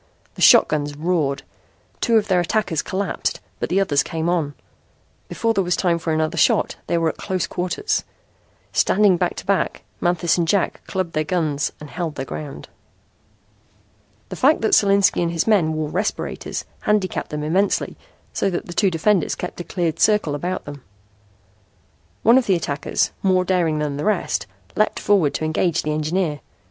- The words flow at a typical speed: Yes, average, 175 wpm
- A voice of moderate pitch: Yes, medium, 175 Hz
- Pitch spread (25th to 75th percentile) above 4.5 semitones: No, average, 3.8 semitones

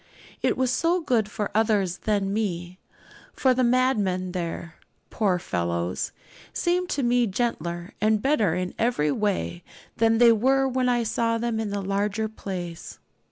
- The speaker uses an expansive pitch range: No, average, 4.8 semitones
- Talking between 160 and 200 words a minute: No, average, 150 wpm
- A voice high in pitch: Yes, high, 215 Hz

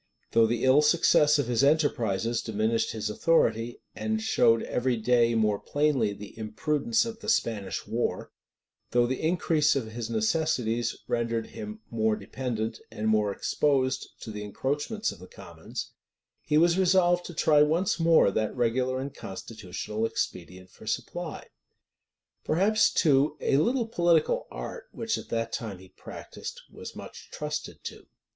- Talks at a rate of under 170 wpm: Yes, average, 150 wpm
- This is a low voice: Yes, low, 125 Hz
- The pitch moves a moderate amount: No, wide, 6.3 semitones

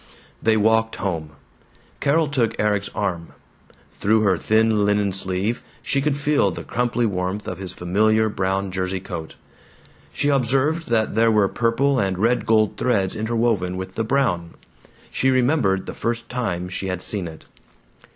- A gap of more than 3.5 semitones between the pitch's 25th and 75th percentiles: Yes, average, 4.0 semitones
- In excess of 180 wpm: No, average, 155 wpm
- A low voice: Yes, low, 110 Hz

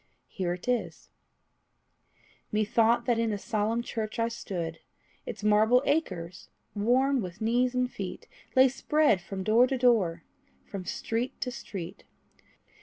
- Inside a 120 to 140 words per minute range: Yes, slow, 135 wpm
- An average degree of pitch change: Yes, average, 4.3 semitones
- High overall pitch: Yes, high, 220 Hz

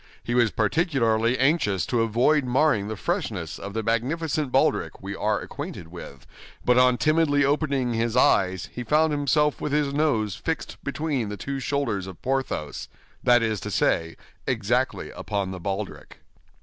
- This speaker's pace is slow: No, average, 155 wpm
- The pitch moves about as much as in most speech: No, wide, 5.7 semitones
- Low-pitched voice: Yes, low, 125 Hz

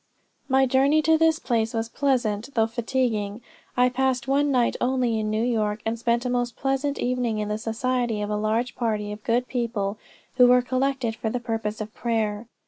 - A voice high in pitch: Yes, high, 240 Hz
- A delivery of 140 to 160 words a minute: No, average, 195 wpm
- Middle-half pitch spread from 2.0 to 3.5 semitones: Yes, average, 2.7 semitones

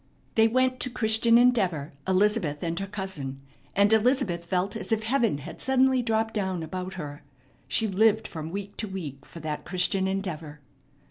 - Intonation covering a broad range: No, average, 4.7 semitones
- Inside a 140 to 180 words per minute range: Yes, average, 170 wpm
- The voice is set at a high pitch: Yes, high, 195 Hz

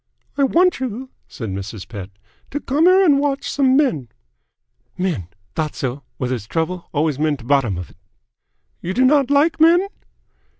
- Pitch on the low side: No, medium, 180 Hz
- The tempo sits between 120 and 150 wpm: No, average, 165 wpm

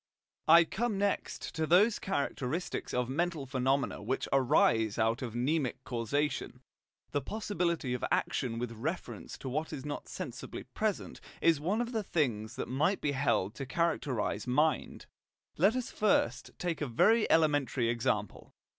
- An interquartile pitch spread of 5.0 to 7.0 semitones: Yes, wide, 5.5 semitones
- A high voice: No, medium, 145 Hz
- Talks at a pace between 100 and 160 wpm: Yes, average, 150 wpm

